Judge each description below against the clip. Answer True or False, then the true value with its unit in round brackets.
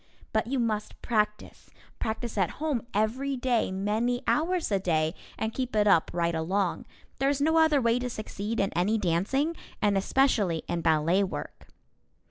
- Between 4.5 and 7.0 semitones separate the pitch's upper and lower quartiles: True (5.1 semitones)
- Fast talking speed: False (165 wpm)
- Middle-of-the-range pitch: False (215 Hz)